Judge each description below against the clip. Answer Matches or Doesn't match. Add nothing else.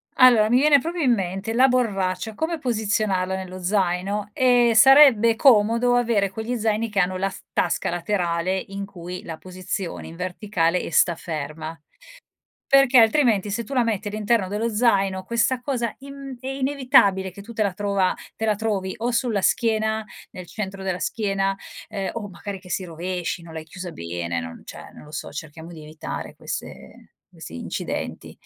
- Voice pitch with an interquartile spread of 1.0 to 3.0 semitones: Doesn't match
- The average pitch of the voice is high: Matches